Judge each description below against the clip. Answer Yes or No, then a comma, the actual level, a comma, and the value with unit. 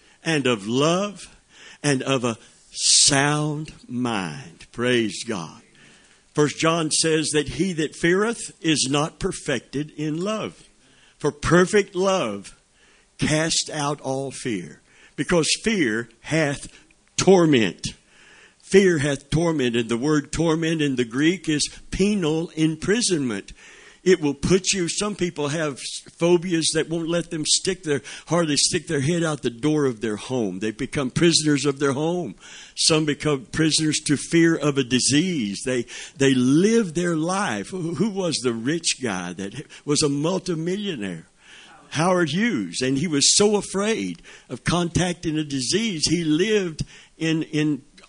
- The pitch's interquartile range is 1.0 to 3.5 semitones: No, average, 3.9 semitones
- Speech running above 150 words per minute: No, average, 140 wpm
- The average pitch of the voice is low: No, medium, 155 Hz